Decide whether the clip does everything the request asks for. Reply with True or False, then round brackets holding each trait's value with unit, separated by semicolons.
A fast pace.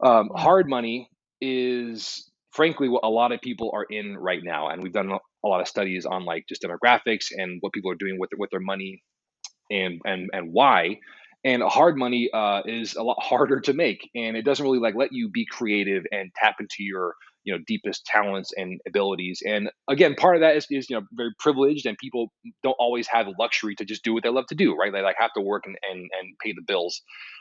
True (240 wpm)